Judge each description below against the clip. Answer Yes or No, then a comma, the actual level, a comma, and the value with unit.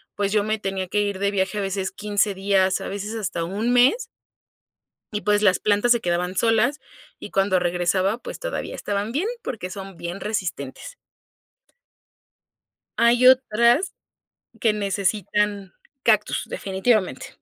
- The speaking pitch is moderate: No, high, 205 Hz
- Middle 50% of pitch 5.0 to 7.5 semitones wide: No, average, 2.7 semitones